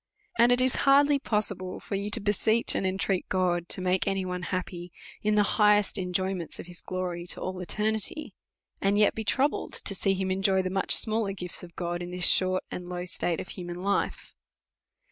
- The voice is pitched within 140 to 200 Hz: Yes, high, 190 Hz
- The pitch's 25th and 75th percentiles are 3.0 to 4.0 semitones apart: No, narrow, 2.5 semitones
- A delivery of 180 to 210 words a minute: Yes, average, 200 wpm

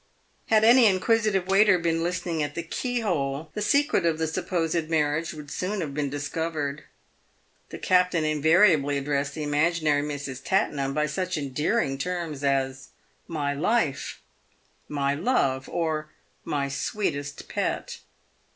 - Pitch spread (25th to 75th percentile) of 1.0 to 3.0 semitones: No, average, 4.2 semitones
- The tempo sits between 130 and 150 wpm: Yes, slow, 135 wpm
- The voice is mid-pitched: Yes, medium, 155 Hz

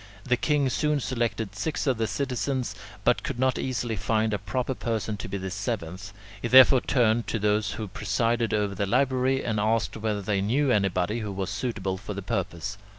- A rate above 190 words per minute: Yes, average, 200 wpm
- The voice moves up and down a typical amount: Yes, average, 3.8 semitones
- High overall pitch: No, low, 110 Hz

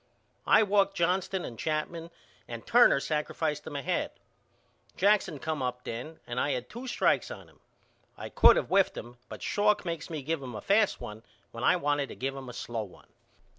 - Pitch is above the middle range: No, medium, 155 Hz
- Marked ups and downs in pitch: Yes, wide, 7.1 semitones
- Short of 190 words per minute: No, average, 195 wpm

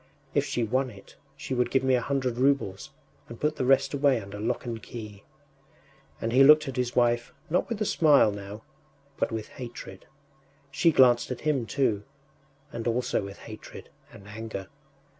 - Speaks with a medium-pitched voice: No, low, 120 Hz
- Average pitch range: Yes, average, 3.6 semitones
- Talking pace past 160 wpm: Yes, average, 180 wpm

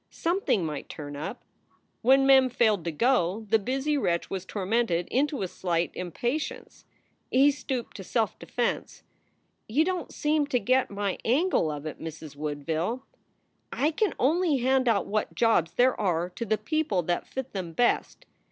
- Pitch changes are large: Yes, wide, 7.3 semitones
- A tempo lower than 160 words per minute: No, average, 165 wpm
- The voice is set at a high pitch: Yes, high, 225 Hz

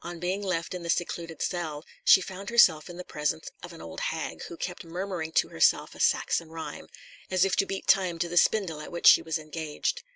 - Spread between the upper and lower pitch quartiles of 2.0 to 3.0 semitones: Yes, narrow, 2.4 semitones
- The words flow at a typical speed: No, fast, 225 wpm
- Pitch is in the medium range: Yes, medium, 170 Hz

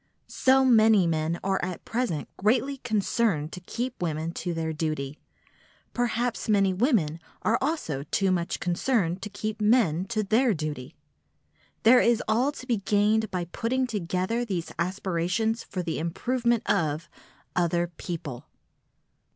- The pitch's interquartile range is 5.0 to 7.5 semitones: Yes, wide, 5.6 semitones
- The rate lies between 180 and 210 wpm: No, slow, 135 wpm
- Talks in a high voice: Yes, high, 195 Hz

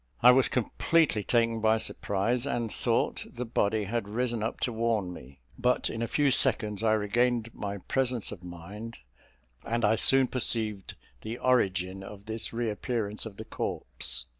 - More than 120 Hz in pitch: No, low, 110 Hz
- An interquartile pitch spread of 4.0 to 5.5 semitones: No, average, 2.8 semitones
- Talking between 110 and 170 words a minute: Yes, average, 165 wpm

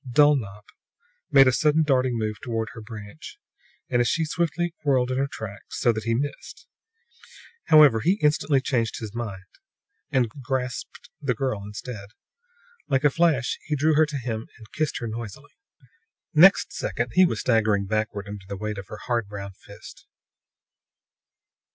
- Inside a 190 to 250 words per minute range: No, average, 160 wpm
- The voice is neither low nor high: No, low, 125 Hz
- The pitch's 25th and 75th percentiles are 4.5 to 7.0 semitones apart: Yes, average, 5.1 semitones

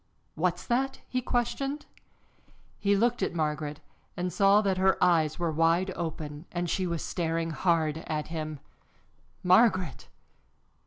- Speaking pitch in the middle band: Yes, medium, 175 Hz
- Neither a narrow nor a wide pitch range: Yes, average, 3.7 semitones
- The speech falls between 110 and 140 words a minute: Yes, slow, 135 wpm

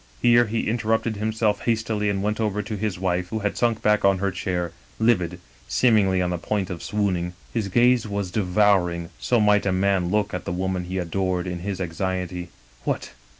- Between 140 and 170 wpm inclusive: No, average, 195 wpm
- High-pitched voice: No, low, 100 Hz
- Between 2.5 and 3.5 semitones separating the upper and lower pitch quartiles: Yes, average, 3.0 semitones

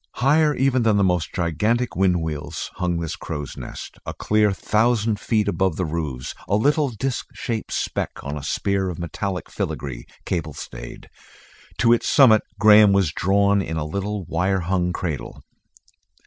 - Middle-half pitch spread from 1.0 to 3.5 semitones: No, average, 4.5 semitones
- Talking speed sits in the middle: Yes, average, 160 wpm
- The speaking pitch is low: Yes, very low, 95 Hz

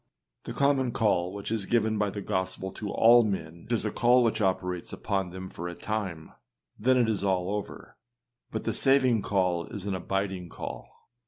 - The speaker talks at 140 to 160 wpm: No, average, 195 wpm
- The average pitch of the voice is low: Yes, low, 100 Hz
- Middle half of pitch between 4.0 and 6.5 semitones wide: No, average, 3.3 semitones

